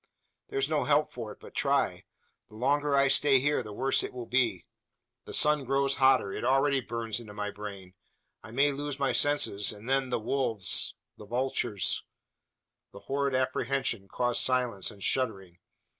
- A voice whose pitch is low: Yes, low, 130 Hz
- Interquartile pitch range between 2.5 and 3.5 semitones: No, average, 4.3 semitones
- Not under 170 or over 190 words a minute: Yes, average, 175 wpm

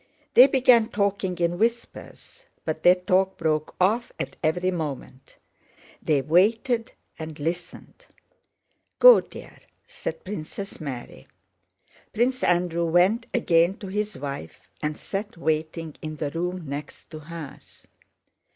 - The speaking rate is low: Yes, slow, 125 wpm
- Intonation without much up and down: No, average, 4.8 semitones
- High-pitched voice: No, medium, 175 Hz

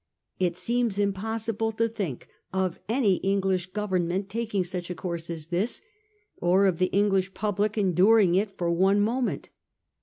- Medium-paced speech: Yes, average, 150 wpm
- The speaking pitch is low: No, high, 195 Hz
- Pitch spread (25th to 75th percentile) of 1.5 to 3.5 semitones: Yes, average, 2.9 semitones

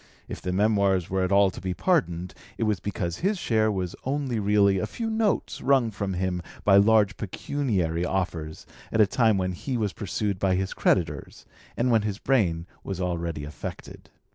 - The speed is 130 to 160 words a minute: No, average, 185 wpm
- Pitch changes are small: No, average, 3.5 semitones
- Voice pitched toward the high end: No, low, 100 Hz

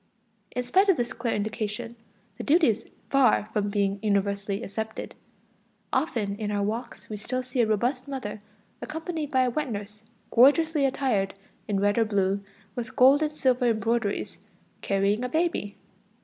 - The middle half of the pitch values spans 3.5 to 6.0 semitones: Yes, average, 4.4 semitones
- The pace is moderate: Yes, average, 160 wpm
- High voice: Yes, high, 230 Hz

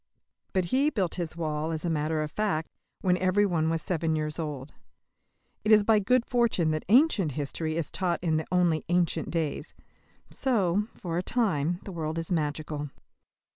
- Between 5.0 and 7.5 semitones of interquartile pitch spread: No, average, 3.7 semitones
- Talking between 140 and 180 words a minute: Yes, average, 175 wpm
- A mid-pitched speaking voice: Yes, medium, 170 Hz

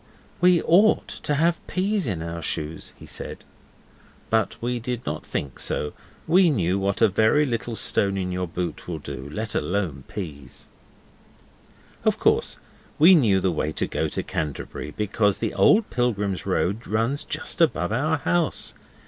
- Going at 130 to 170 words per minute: Yes, average, 160 wpm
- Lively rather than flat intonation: Yes, wide, 8.2 semitones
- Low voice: Yes, low, 105 Hz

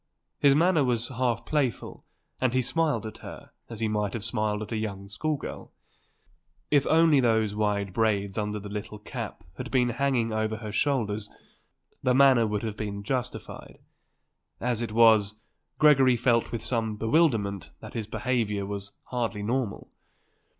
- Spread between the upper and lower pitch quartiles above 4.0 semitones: No, average, 3.4 semitones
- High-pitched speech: No, low, 115 Hz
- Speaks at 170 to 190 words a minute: No, average, 160 wpm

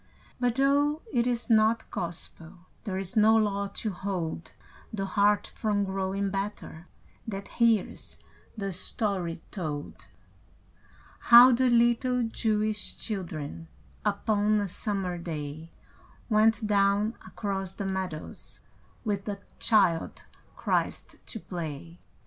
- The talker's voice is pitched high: Yes, high, 200 Hz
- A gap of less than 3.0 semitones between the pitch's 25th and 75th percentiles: No, average, 3.3 semitones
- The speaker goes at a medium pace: No, slow, 115 wpm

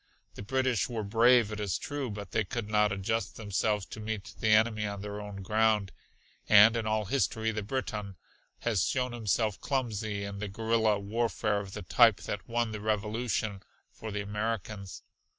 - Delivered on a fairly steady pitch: Yes, narrow, 1.9 semitones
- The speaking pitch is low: Yes, low, 110 Hz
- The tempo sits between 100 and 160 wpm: No, average, 175 wpm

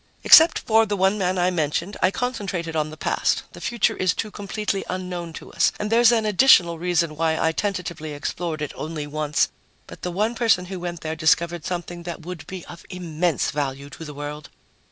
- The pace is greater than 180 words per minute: Yes, average, 200 wpm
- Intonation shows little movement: No, average, 3.7 semitones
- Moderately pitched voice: Yes, medium, 175 Hz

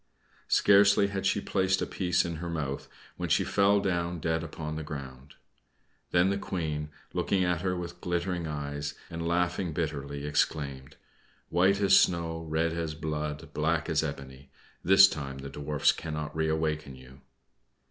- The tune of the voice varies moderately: Yes, average, 3.0 semitones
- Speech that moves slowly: No, average, 155 wpm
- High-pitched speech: No, very low, 80 Hz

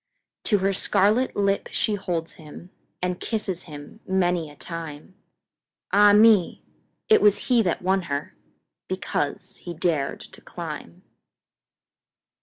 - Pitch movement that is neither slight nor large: Yes, average, 3.4 semitones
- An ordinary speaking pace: No, slow, 110 wpm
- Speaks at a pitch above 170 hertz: Yes, medium, 185 Hz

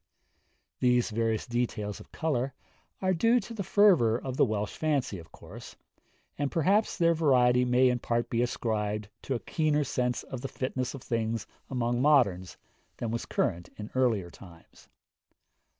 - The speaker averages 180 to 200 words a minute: No, average, 160 wpm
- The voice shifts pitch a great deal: No, average, 4.1 semitones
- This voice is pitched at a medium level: No, low, 125 Hz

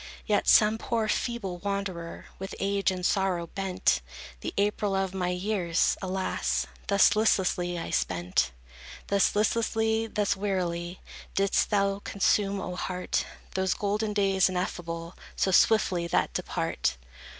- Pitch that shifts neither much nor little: No, narrow, 2.3 semitones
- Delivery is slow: Yes, slow, 130 wpm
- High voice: Yes, high, 195 Hz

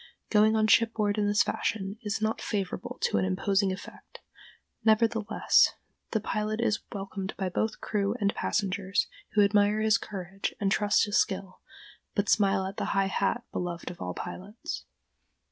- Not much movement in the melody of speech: Yes, narrow, 1.9 semitones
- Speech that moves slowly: No, average, 160 wpm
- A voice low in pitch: No, high, 205 Hz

